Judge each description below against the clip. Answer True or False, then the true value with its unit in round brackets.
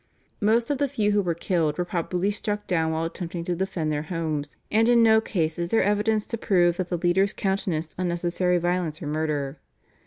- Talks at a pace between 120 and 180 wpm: False (205 wpm)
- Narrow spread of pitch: False (4.0 semitones)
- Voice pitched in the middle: True (175 Hz)